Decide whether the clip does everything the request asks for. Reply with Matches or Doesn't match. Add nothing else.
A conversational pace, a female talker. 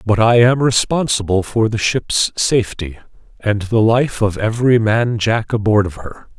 Doesn't match